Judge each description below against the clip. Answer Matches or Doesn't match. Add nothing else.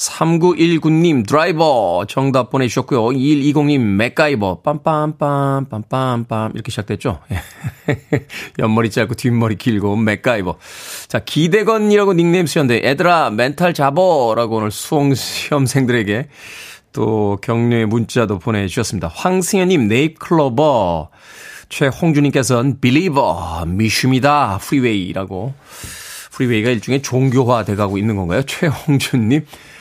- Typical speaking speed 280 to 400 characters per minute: Matches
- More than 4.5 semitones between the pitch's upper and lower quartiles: Matches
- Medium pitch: Doesn't match